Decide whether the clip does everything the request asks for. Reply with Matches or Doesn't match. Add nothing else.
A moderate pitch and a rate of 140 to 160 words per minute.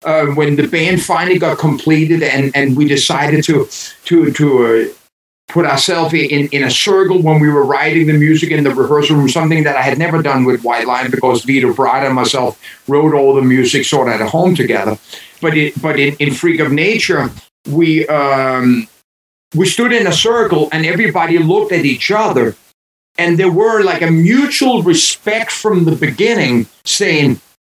Doesn't match